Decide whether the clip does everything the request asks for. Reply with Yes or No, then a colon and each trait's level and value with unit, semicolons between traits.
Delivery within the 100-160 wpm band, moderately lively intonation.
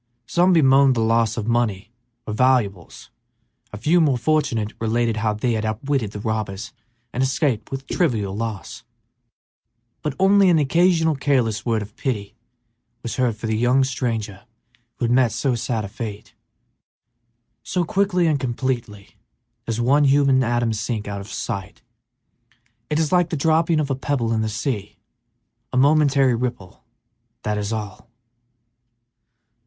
Yes: average, 150 wpm; average, 4.5 semitones